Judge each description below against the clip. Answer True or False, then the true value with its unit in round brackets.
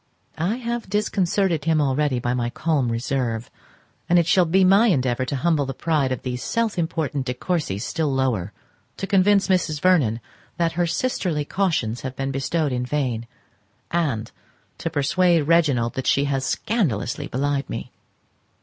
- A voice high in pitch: False (150 Hz)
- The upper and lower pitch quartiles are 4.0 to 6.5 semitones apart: True (5.4 semitones)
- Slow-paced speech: False (160 wpm)